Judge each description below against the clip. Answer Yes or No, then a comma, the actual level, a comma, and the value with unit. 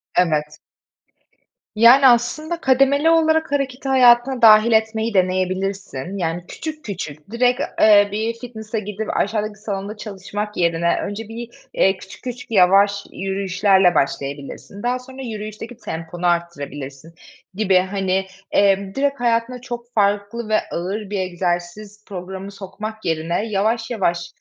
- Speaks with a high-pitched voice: Yes, high, 205 Hz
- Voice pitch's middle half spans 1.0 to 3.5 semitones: No, average, 4.0 semitones